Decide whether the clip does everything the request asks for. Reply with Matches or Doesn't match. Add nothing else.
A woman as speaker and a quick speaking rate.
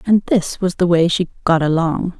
Matches